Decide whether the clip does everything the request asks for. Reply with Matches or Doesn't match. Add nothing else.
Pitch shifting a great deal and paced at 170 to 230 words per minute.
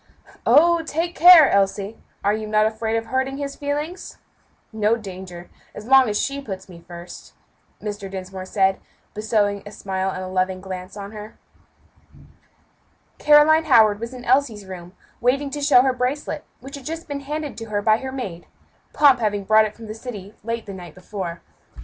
Matches